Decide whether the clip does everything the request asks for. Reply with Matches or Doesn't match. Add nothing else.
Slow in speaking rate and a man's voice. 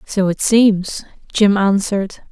Doesn't match